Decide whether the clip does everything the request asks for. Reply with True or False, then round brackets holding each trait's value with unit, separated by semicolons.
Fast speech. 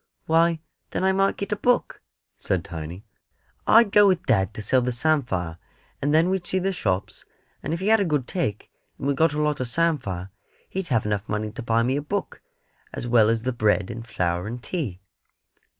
True (210 wpm)